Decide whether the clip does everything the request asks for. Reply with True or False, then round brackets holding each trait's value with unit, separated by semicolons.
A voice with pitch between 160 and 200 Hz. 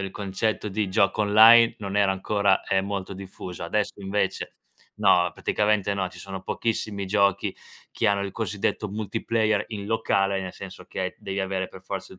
False (100 Hz)